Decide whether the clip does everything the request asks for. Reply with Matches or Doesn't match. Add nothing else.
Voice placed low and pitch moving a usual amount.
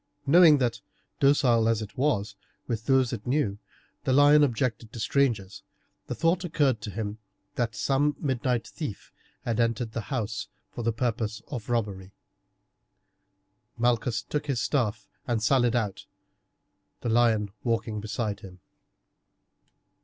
Matches